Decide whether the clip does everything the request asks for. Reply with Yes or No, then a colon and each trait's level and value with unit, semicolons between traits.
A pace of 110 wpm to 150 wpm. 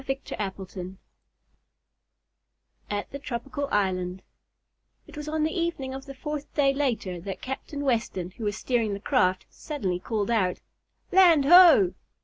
Yes: average, 140 wpm